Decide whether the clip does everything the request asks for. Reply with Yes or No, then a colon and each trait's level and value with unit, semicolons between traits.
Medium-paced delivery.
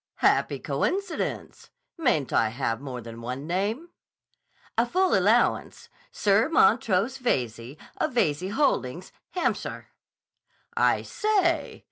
No: slow, 105 wpm